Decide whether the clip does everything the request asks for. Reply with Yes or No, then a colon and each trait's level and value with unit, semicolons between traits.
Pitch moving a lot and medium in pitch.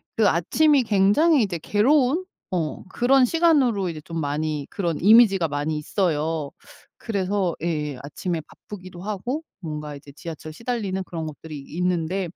Yes: wide, 5.9 semitones; medium, 180 Hz